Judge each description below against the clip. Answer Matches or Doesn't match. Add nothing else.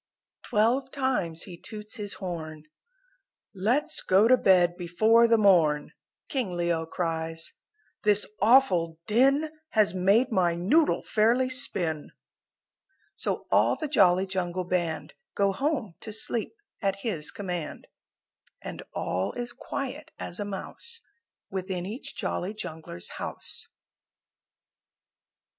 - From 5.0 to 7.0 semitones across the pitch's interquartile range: Matches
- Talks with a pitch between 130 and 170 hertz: Doesn't match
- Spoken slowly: Matches